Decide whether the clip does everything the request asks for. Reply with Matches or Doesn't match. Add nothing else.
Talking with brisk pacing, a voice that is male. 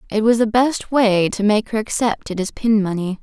Doesn't match